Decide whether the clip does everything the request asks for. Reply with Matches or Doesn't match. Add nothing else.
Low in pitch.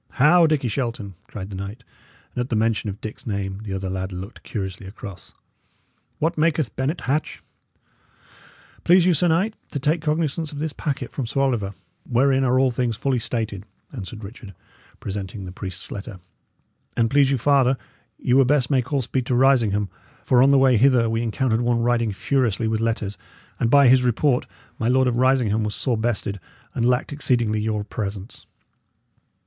Matches